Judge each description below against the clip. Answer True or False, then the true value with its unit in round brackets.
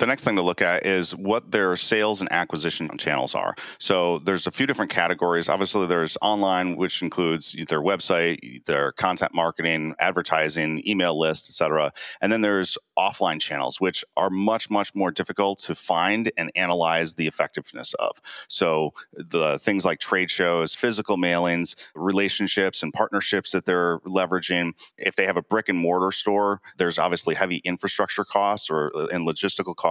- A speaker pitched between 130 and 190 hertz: False (90 Hz)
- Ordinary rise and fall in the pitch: True (3.0 semitones)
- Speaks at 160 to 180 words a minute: True (170 wpm)